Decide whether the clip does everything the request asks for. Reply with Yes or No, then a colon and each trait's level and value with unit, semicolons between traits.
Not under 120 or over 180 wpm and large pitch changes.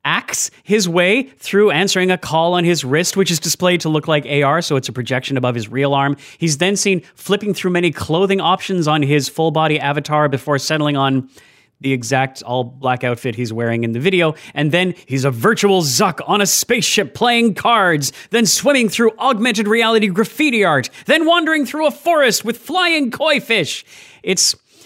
No: average, 190 wpm; wide, 7.4 semitones